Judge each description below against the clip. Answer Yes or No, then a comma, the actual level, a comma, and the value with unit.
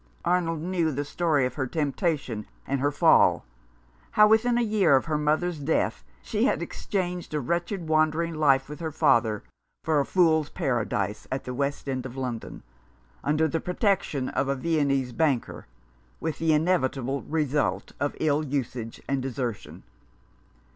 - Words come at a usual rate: Yes, average, 160 wpm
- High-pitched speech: No, medium, 150 Hz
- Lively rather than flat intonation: No, average, 3.7 semitones